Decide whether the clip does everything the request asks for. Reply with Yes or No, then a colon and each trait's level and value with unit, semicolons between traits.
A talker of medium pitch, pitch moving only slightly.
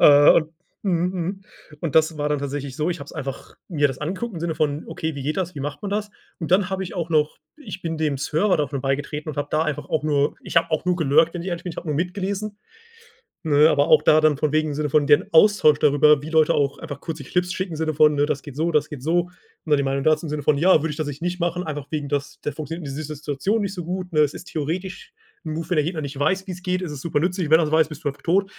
No: medium, 155 Hz; average, 3.3 semitones